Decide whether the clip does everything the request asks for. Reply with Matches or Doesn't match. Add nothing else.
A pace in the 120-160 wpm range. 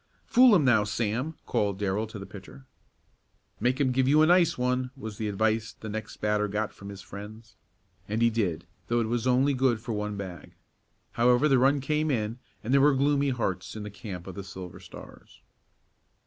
Doesn't match